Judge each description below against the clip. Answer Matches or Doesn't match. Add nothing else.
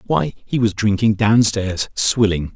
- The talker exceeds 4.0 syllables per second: Doesn't match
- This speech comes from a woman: Doesn't match